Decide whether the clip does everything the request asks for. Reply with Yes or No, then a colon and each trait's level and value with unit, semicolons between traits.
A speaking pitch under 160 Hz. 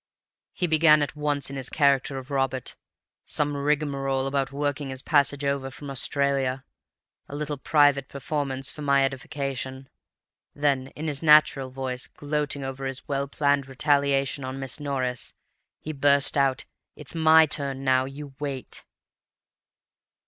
Yes: medium, 140 Hz